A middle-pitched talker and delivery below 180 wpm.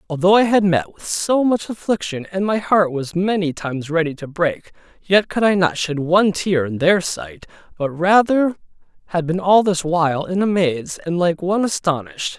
No: medium, 175 Hz; average, 200 wpm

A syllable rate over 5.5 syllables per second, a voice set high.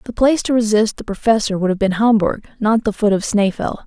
Yes: 5.9 syllables/s; high, 215 Hz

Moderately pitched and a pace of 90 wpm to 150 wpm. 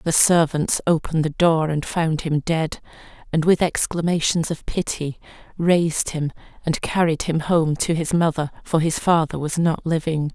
No: medium, 160 Hz; average, 170 wpm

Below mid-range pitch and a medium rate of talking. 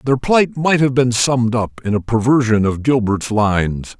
Yes: low, 120 Hz; average, 195 wpm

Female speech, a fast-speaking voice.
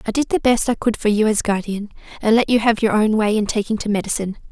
Yes: female; fast, 280 wpm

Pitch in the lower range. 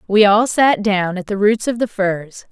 No: high, 205 Hz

